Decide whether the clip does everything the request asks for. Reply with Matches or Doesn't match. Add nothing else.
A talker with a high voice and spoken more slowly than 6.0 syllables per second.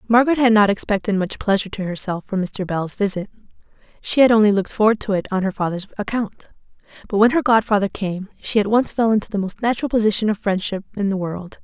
Doesn't match